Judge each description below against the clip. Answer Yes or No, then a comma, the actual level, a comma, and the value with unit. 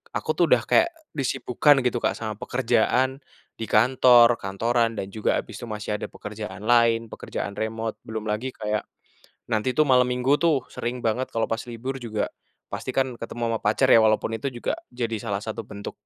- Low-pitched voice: Yes, low, 115 Hz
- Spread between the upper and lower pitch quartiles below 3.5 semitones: Yes, narrow, 2.6 semitones